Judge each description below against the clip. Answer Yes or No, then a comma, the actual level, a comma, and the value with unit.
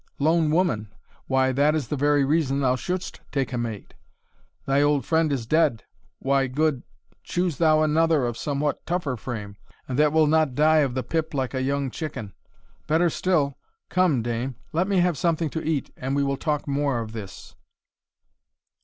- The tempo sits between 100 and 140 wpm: No, average, 180 wpm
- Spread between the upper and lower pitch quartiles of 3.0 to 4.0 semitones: Yes, average, 3.3 semitones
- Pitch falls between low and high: Yes, medium, 145 Hz